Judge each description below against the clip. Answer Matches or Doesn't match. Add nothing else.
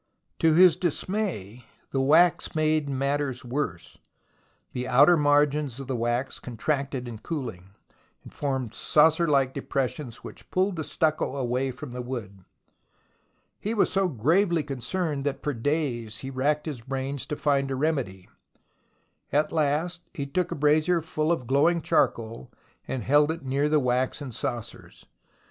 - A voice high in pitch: Doesn't match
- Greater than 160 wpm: Doesn't match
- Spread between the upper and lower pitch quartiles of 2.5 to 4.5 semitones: Matches